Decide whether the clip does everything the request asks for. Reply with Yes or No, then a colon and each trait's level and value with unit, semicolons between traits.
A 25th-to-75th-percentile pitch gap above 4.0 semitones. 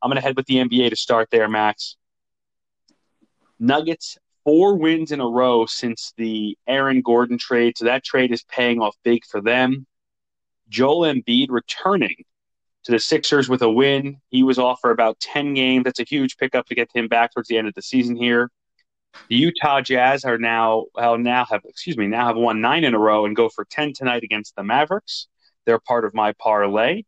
No: narrow, 2.5 semitones